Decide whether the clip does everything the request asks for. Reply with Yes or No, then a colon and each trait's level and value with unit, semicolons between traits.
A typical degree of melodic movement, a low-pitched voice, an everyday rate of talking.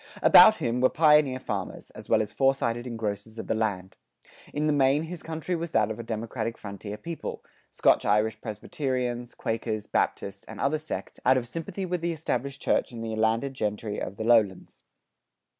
Yes: average, 4.9 semitones; low, 120 Hz; average, 180 wpm